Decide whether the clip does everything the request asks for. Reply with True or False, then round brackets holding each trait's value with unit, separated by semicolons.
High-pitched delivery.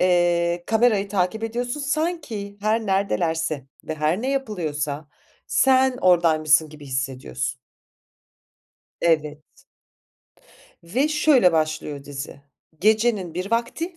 False (180 Hz)